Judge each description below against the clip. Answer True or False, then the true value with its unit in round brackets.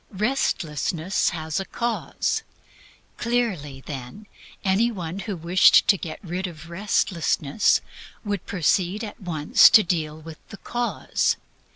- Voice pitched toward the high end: False (180 Hz)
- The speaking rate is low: True (125 wpm)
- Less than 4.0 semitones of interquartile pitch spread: False (4.7 semitones)